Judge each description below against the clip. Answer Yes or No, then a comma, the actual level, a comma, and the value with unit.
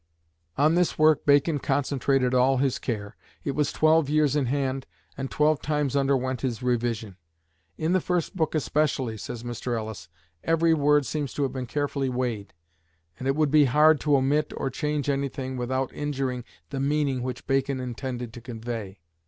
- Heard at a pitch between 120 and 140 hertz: Yes, low, 135 Hz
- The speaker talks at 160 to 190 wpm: Yes, average, 170 wpm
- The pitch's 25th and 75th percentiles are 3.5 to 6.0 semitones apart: No, average, 2.9 semitones